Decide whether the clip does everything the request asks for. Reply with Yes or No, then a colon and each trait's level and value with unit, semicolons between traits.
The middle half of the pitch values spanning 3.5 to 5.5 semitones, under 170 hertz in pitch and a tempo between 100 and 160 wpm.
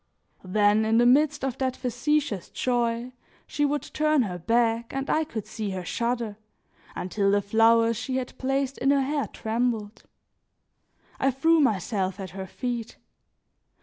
No: average, 4.1 semitones; high, 235 Hz; average, 150 wpm